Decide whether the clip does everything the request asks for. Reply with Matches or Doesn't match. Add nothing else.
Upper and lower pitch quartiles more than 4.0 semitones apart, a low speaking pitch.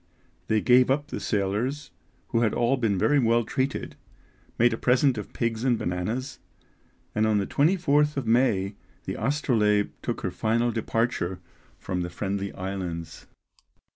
Matches